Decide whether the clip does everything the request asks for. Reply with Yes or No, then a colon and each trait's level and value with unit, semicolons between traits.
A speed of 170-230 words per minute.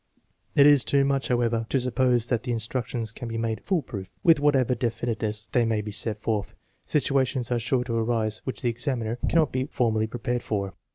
Yes: fast, 205 wpm